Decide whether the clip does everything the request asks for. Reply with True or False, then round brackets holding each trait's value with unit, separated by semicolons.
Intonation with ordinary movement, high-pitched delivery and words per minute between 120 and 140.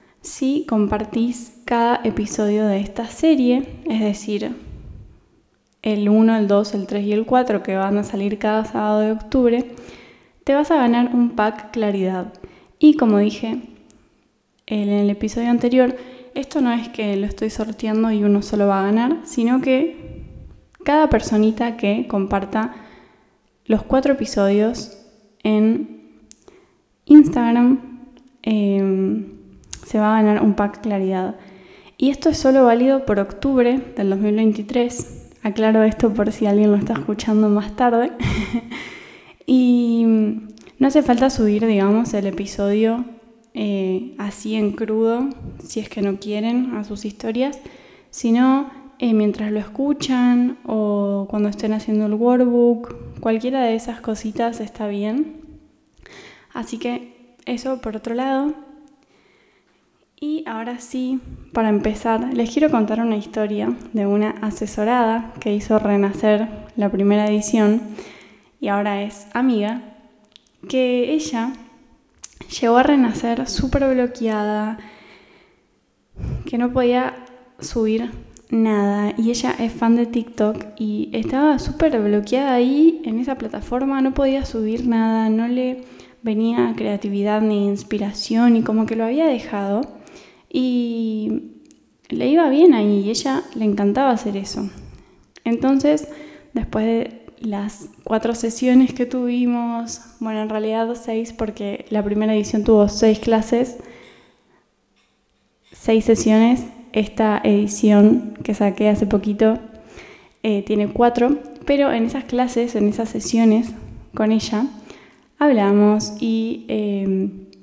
True (3.0 semitones; 225 Hz; 130 wpm)